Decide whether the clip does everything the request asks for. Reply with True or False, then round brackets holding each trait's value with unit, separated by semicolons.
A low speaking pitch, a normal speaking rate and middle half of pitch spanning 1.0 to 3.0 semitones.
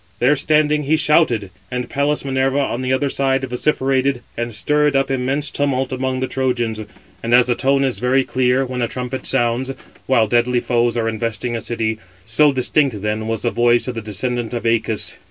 True (125 Hz; 190 wpm; 2.4 semitones)